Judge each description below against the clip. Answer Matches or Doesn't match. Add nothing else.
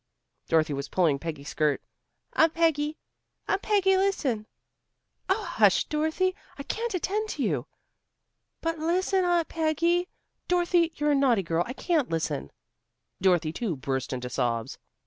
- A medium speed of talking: Matches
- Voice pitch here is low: Doesn't match